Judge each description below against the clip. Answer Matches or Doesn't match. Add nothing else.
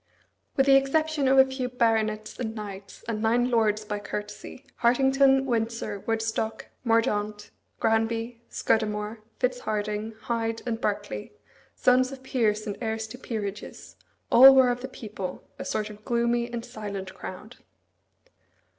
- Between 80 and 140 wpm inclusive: Matches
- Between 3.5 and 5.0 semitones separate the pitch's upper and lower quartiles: Doesn't match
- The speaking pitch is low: Doesn't match